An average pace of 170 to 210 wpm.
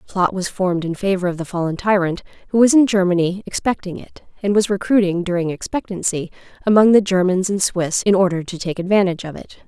Yes: fast, 205 wpm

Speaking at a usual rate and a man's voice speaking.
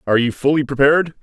Yes: average, 195 wpm; male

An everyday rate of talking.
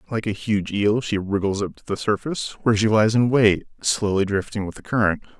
No: fast, 220 wpm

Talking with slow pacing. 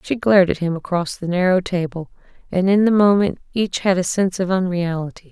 No: fast, 205 wpm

